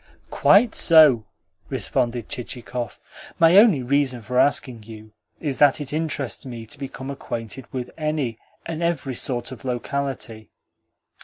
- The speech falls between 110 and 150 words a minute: Yes, slow, 135 wpm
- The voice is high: No, low, 130 Hz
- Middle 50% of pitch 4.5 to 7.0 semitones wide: No, average, 3.5 semitones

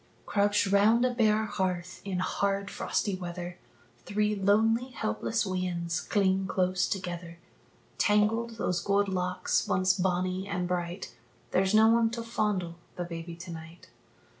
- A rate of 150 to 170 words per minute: No, average, 140 wpm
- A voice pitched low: No, high, 190 Hz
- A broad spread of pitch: No, average, 2.7 semitones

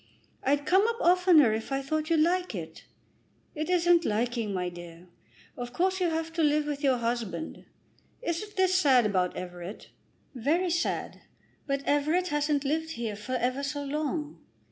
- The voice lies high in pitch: Yes, very high, 290 Hz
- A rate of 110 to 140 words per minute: No, average, 165 wpm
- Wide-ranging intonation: Yes, wide, 5.8 semitones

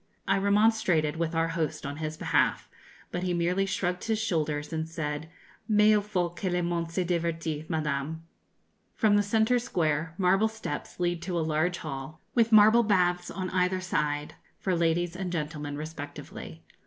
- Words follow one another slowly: No, average, 165 wpm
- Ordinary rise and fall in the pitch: Yes, average, 3.5 semitones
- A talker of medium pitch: Yes, medium, 175 Hz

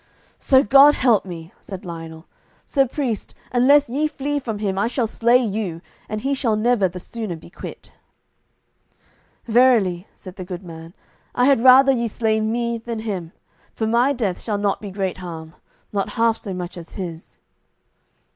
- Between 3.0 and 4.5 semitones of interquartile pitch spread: No, average, 5.1 semitones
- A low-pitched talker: No, high, 220 Hz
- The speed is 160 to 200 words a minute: Yes, average, 170 wpm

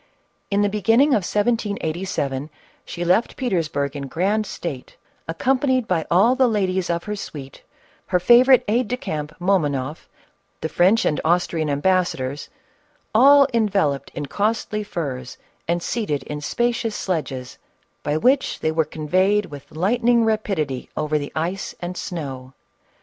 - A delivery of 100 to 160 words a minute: Yes, average, 140 wpm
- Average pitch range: No, wide, 6.2 semitones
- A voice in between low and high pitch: Yes, medium, 180 Hz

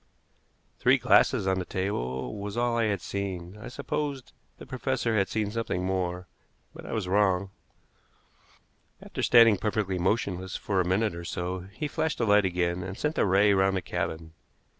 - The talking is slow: No, average, 175 wpm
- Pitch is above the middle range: No, very low, 95 Hz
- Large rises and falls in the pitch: No, average, 3.2 semitones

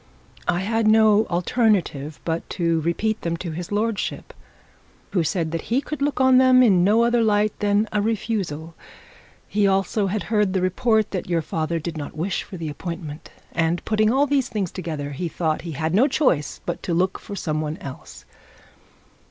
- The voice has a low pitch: No, high, 190 Hz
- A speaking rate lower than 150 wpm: No, average, 185 wpm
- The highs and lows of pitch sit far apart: No, average, 4.7 semitones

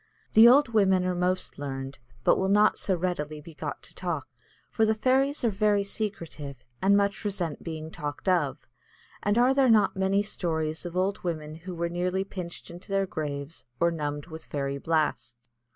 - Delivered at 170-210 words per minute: Yes, average, 185 wpm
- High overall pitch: No, medium, 180 Hz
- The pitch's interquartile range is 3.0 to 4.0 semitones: No, average, 4.5 semitones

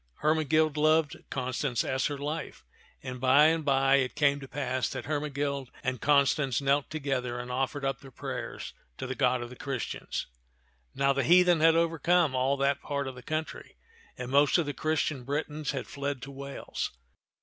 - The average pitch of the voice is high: No, medium, 140 Hz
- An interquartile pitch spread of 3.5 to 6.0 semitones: No, narrow, 2.4 semitones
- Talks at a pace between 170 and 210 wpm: Yes, average, 180 wpm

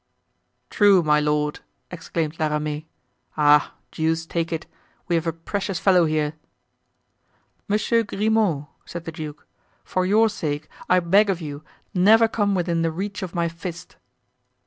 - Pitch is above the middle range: No, medium, 170 Hz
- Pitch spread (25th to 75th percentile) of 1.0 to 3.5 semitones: No, average, 4.0 semitones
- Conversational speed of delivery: Yes, average, 145 wpm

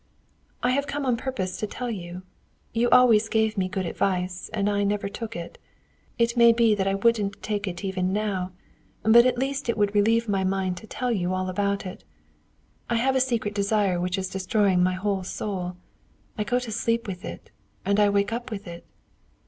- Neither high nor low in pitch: No, high, 205 Hz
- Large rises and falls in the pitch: No, average, 3.6 semitones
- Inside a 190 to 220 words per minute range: Yes, fast, 205 wpm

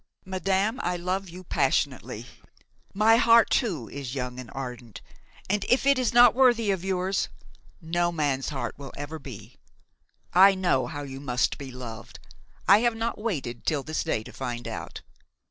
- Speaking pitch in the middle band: Yes, medium, 175 Hz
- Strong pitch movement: Yes, wide, 7.4 semitones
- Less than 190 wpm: Yes, average, 165 wpm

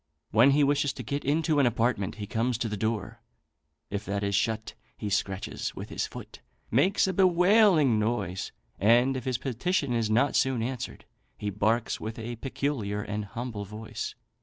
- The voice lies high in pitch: No, low, 115 Hz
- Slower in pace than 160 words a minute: No, average, 175 wpm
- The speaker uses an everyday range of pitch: Yes, average, 4.6 semitones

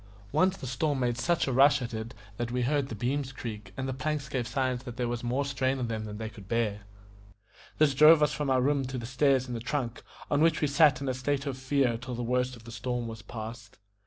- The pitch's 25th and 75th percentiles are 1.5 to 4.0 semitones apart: Yes, average, 2.8 semitones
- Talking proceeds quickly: Yes, fast, 255 wpm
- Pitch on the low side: Yes, low, 130 Hz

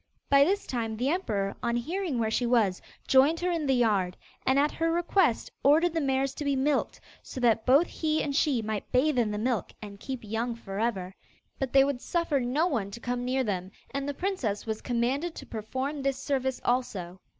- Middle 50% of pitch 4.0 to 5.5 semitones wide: Yes, average, 4.5 semitones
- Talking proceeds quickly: Yes, fast, 210 wpm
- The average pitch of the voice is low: No, very high, 260 Hz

